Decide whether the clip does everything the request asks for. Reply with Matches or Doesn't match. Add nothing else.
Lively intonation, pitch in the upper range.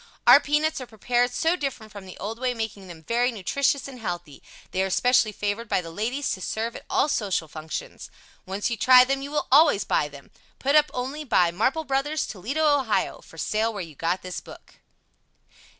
Matches